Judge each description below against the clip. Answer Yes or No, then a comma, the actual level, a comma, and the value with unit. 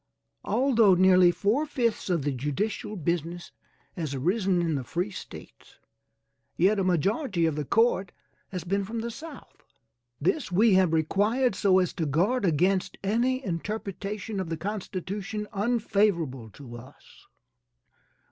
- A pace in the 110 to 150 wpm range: Yes, average, 140 wpm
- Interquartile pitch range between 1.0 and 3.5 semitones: No, average, 4.2 semitones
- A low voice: No, high, 190 Hz